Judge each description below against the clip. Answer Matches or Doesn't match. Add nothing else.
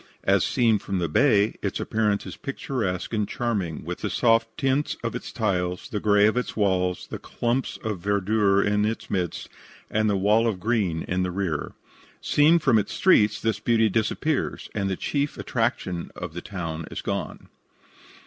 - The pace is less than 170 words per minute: Doesn't match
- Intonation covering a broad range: Doesn't match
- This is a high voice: Doesn't match